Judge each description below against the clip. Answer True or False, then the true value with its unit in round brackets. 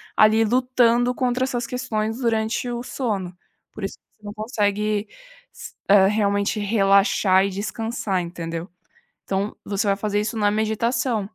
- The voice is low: False (215 Hz)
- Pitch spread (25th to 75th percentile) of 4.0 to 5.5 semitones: False (2.7 semitones)